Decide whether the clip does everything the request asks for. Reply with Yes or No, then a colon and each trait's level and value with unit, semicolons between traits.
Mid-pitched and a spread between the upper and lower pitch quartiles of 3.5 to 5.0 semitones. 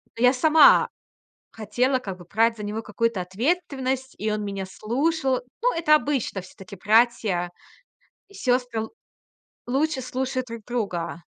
No: high, 235 Hz; average, 4.2 semitones